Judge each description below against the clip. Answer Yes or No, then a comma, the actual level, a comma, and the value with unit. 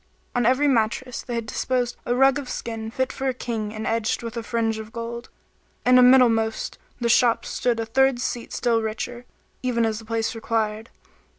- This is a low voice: No, high, 235 Hz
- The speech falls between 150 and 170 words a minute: No, average, 195 wpm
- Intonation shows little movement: Yes, narrow, 1.9 semitones